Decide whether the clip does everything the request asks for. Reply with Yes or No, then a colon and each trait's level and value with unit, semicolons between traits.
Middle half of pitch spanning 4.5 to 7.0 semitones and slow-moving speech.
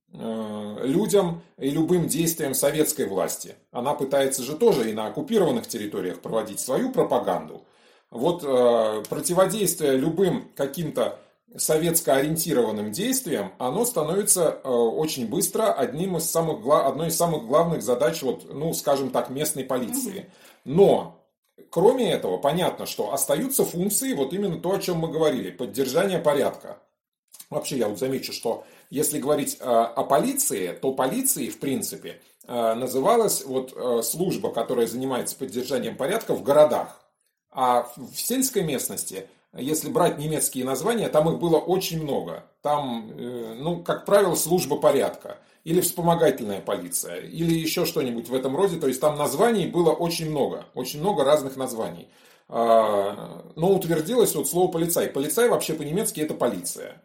No: average, 5.3 semitones; average, 135 wpm